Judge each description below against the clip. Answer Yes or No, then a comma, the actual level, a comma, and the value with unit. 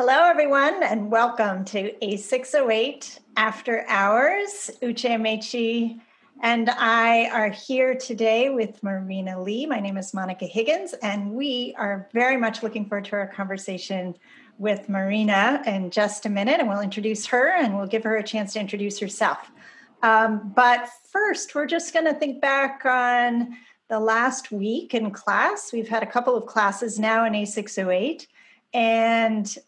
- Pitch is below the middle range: No, high, 225 Hz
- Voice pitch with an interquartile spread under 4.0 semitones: Yes, average, 3.2 semitones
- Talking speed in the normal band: Yes, average, 170 wpm